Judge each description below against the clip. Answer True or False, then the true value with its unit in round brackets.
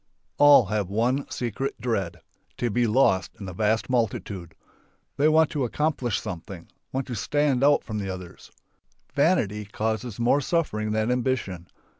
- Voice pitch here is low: True (115 Hz)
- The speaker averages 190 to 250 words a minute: False (150 wpm)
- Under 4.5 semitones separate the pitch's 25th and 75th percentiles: False (4.9 semitones)